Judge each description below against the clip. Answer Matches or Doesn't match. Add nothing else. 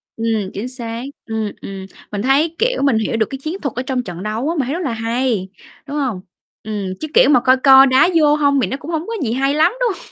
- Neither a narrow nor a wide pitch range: Matches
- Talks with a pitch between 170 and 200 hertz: Doesn't match